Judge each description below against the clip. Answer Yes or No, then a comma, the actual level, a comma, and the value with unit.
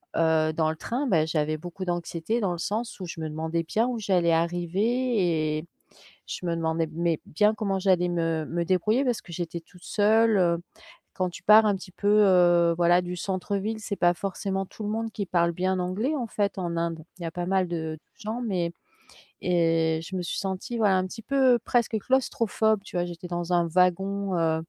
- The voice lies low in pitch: No, medium, 180 Hz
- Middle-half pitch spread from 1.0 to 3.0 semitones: No, average, 3.6 semitones